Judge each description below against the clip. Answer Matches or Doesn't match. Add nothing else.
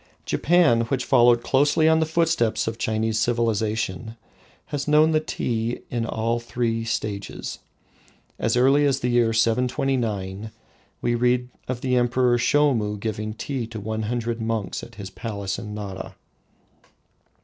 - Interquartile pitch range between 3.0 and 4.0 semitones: Doesn't match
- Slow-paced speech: Doesn't match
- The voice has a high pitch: Doesn't match